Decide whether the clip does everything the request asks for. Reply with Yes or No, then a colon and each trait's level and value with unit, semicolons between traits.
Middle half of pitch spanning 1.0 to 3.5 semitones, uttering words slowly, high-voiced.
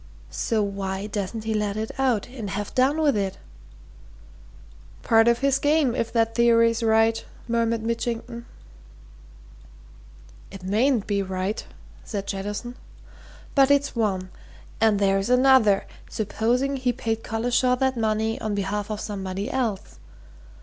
Yes: average, 3.2 semitones; slow, 130 wpm; high, 225 Hz